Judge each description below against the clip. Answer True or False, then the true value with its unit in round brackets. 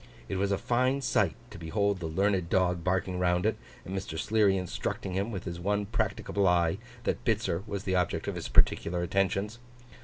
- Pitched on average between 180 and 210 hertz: False (95 Hz)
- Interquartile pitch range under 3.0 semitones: True (2.5 semitones)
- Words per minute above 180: True (190 wpm)